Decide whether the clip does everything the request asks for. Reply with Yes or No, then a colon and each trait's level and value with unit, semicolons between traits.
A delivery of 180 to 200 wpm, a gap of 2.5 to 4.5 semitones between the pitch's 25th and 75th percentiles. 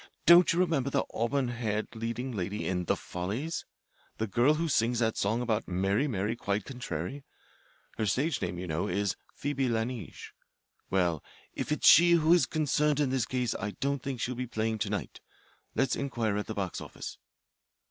No: average, 185 wpm; average, 5.2 semitones